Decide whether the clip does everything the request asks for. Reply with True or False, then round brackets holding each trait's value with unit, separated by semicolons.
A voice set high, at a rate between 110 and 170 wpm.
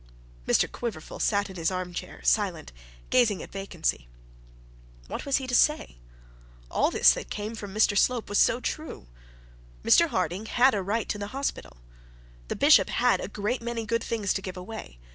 False (205 Hz; 180 wpm)